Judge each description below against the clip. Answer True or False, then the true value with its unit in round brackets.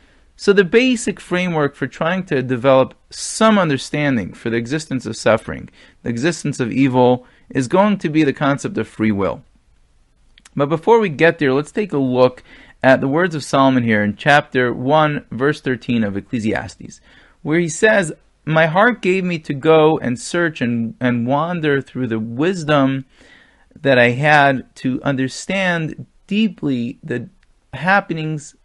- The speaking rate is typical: True (155 wpm)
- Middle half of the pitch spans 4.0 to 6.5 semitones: True (4.8 semitones)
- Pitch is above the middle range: False (140 Hz)